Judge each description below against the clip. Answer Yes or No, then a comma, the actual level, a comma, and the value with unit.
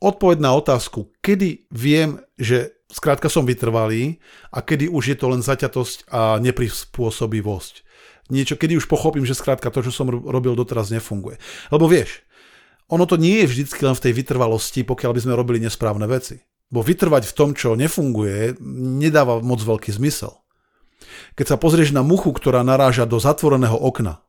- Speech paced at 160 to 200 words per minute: Yes, fast, 165 wpm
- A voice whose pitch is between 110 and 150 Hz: Yes, low, 130 Hz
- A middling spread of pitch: Yes, average, 3.9 semitones